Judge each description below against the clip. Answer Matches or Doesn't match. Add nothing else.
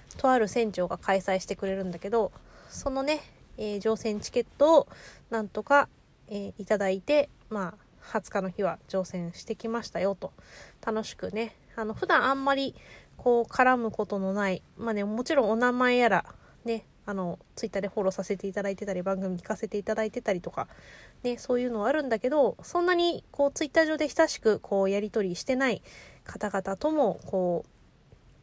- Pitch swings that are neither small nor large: Matches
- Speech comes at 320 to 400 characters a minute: Matches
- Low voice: Doesn't match